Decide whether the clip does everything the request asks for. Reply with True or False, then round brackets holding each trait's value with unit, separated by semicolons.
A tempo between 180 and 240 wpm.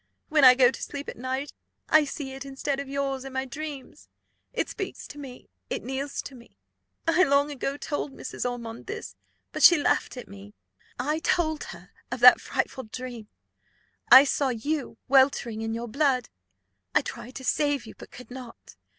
True (185 wpm)